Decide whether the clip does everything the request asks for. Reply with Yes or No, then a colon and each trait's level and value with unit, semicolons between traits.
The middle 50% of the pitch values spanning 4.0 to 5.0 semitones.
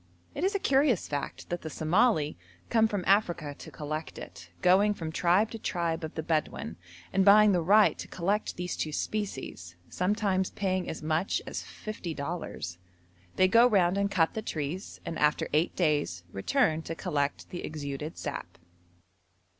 Yes: average, 4.7 semitones